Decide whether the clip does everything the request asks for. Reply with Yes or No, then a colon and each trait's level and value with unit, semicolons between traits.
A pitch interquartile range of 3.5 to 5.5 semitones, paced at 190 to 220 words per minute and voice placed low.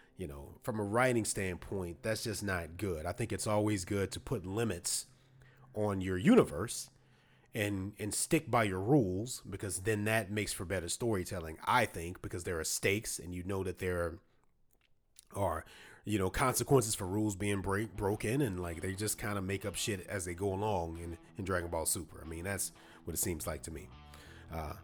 Yes: average, 3.8 semitones; average, 200 wpm; low, 100 Hz